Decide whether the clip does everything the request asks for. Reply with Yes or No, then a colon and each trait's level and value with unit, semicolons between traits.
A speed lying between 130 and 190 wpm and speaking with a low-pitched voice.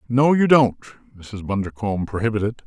Yes: slow, 135 wpm; low, 110 Hz